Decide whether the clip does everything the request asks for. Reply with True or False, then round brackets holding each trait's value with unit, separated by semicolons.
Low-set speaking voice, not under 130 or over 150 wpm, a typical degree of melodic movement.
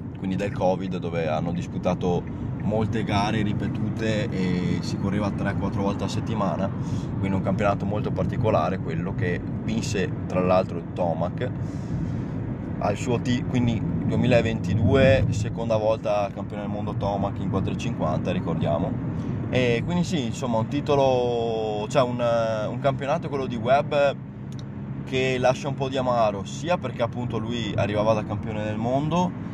True (110 Hz; 140 wpm; 4.2 semitones)